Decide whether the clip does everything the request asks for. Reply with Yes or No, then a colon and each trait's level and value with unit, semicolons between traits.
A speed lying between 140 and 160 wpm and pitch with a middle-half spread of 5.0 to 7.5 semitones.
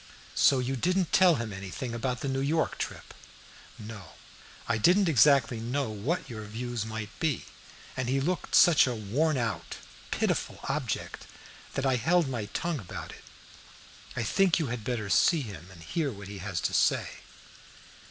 No: average, 170 wpm; wide, 5.6 semitones